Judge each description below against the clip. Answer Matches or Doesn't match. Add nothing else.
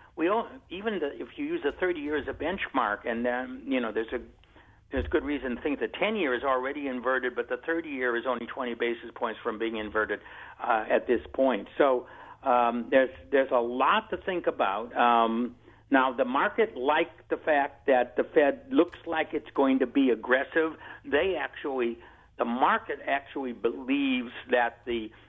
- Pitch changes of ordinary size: Matches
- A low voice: Matches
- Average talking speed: Matches